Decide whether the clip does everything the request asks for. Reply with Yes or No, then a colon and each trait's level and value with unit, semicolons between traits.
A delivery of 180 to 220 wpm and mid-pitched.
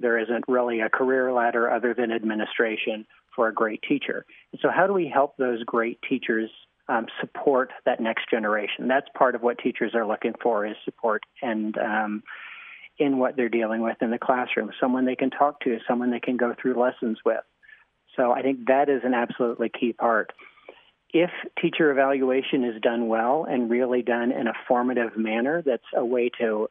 No: average, 190 wpm; low, 120 Hz